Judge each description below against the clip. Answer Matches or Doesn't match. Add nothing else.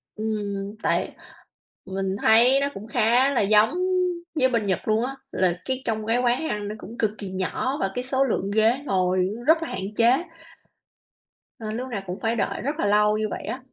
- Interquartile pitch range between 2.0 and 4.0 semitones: Matches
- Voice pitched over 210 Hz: Matches